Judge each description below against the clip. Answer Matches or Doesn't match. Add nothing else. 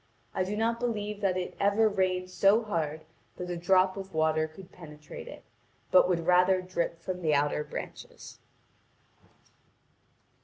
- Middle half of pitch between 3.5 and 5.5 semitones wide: Doesn't match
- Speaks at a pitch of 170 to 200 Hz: Matches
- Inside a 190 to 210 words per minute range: Doesn't match